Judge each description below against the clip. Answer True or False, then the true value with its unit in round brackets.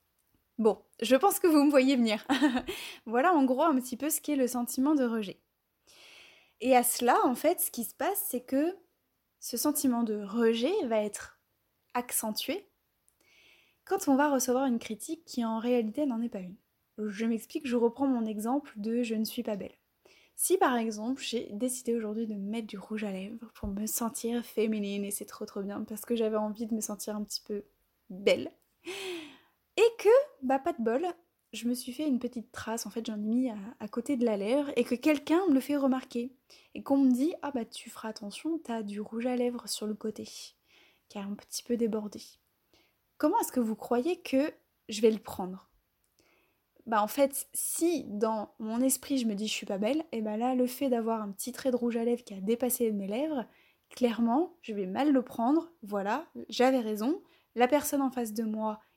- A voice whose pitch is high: True (240 Hz)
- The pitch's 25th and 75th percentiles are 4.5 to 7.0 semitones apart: False (4.0 semitones)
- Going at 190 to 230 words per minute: True (210 wpm)